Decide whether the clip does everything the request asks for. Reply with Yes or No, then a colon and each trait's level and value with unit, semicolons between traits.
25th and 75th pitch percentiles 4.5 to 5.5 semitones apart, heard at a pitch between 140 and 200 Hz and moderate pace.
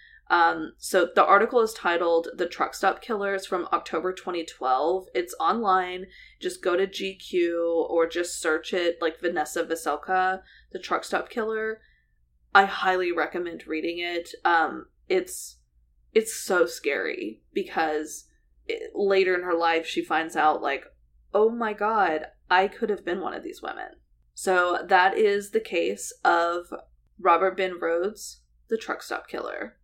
Yes: average, 4.9 semitones; medium, 185 Hz; average, 150 wpm